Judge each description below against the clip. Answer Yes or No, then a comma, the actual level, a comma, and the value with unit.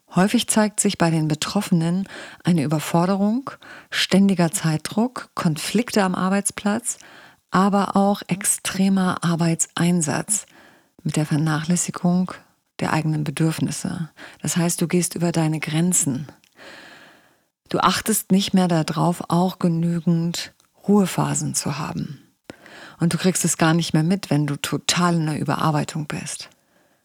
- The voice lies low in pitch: No, medium, 175 Hz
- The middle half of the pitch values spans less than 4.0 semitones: Yes, average, 3.2 semitones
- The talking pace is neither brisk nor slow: No, slow, 120 wpm